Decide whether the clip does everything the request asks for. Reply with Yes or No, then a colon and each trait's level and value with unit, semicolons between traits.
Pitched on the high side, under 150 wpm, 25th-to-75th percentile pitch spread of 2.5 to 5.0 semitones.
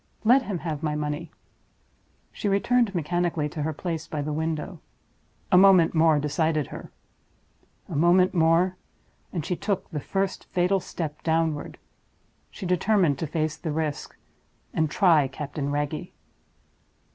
No: medium, 160 Hz; average, 140 wpm; average, 3.2 semitones